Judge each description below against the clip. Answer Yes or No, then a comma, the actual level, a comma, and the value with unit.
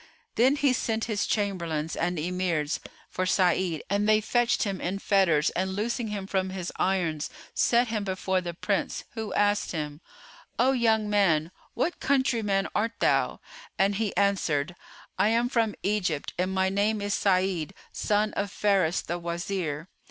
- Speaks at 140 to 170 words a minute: Yes, average, 160 wpm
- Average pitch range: Yes, average, 3.3 semitones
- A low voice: No, high, 195 Hz